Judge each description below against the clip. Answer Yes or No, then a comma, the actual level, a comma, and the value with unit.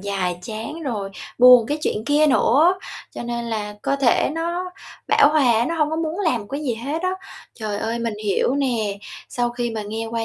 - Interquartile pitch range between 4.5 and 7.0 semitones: Yes, average, 5.3 semitones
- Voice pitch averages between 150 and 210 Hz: No, high, 240 Hz